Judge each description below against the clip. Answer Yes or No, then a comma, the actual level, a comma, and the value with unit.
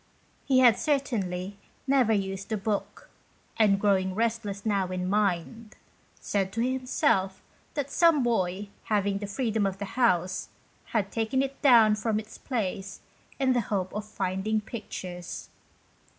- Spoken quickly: No, average, 140 wpm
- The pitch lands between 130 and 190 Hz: No, high, 210 Hz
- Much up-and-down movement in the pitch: No, average, 3.5 semitones